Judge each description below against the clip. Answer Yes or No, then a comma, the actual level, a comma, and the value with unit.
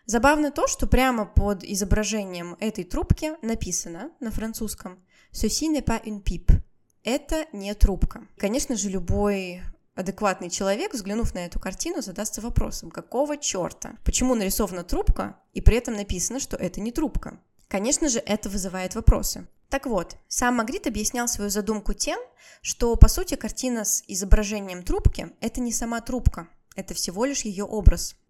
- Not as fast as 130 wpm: No, average, 155 wpm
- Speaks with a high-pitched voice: Yes, high, 220 Hz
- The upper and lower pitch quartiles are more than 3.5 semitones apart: Yes, average, 4.2 semitones